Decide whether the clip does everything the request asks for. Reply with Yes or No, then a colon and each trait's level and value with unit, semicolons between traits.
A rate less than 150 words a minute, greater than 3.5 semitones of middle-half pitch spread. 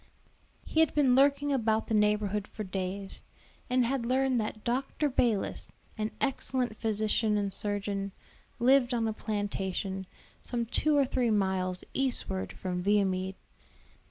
Yes: slow, 135 wpm; average, 4.3 semitones